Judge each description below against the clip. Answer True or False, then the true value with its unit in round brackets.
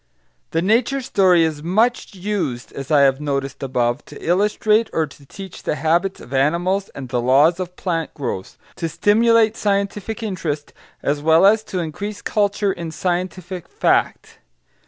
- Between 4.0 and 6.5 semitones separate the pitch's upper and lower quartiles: True (5.6 semitones)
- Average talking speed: True (155 wpm)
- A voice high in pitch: False (175 Hz)